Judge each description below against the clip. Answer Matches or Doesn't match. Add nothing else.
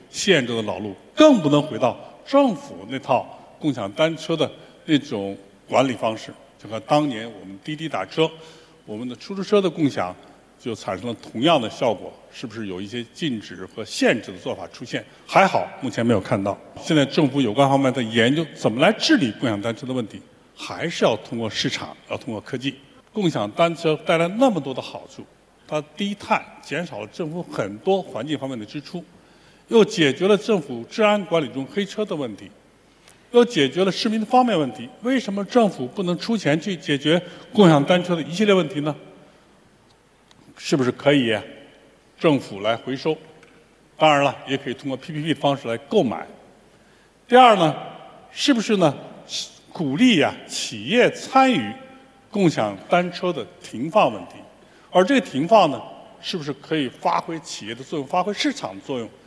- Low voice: Doesn't match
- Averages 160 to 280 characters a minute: Matches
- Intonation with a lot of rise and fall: Matches